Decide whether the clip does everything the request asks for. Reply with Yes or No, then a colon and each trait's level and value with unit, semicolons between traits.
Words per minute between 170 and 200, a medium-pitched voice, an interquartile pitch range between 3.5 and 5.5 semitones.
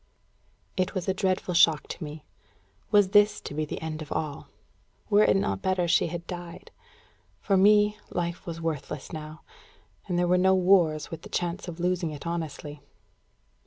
No: average, 175 wpm; medium, 175 Hz; average, 3.1 semitones